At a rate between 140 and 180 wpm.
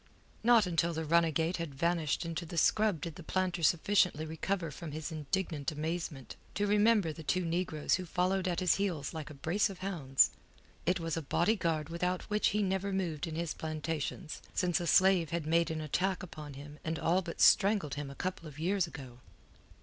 No: average, 195 wpm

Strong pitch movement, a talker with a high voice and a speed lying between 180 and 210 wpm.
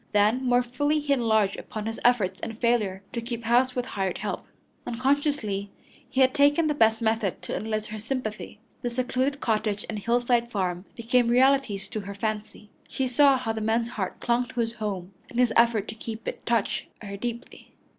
No: average, 2.8 semitones; high, 230 Hz; average, 190 wpm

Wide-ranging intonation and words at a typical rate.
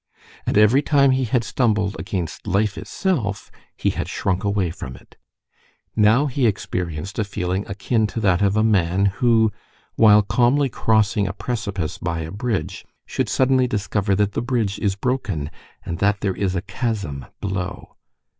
No: average, 3.3 semitones; average, 165 wpm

